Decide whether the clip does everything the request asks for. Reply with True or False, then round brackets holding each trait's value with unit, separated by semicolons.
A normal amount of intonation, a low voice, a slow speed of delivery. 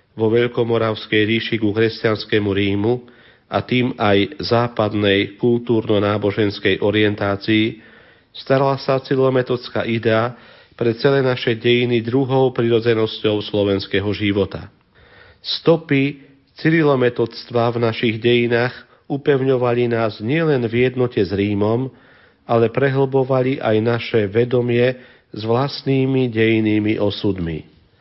True (3.0 semitones; 115 Hz; 95 wpm)